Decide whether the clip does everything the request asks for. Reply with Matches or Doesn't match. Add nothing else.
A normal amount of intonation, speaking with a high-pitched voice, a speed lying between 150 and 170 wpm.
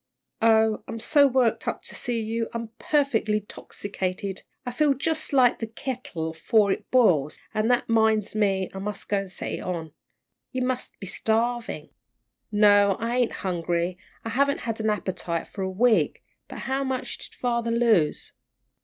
Matches